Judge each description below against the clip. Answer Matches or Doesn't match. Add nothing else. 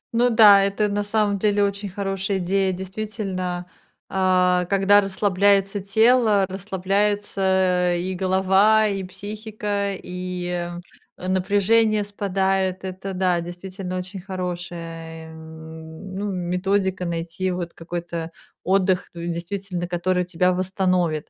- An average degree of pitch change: Doesn't match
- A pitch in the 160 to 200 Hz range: Matches